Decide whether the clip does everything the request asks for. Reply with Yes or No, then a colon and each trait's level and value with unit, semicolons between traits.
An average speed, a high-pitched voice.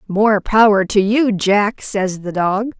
Yes: average, 170 wpm; high, 205 Hz